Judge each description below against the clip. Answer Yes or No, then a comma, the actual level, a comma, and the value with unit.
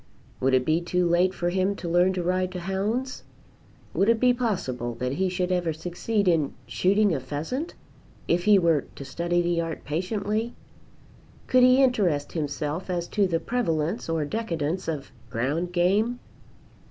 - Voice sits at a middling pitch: Yes, medium, 180 Hz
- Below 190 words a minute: Yes, average, 165 wpm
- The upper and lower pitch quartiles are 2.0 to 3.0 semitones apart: No, average, 3.9 semitones